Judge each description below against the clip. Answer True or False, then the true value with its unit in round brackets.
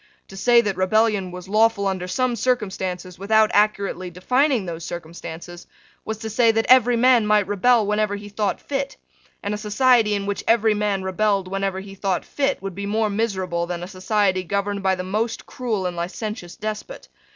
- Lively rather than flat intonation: False (3.0 semitones)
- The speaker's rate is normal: True (185 wpm)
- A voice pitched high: True (205 Hz)